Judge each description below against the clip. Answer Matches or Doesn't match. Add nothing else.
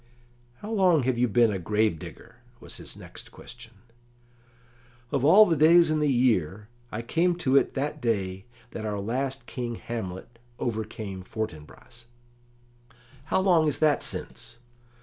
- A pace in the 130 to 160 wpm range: Matches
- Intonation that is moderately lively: Doesn't match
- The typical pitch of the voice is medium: Doesn't match